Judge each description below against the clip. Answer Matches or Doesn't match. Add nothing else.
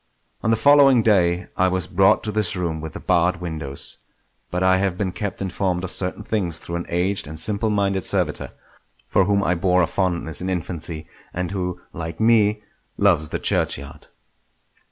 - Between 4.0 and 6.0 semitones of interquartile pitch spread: Doesn't match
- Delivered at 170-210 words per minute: Matches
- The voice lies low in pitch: Matches